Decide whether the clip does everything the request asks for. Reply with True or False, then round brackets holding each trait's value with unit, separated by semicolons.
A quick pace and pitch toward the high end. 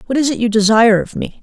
True (295 wpm; 230 Hz)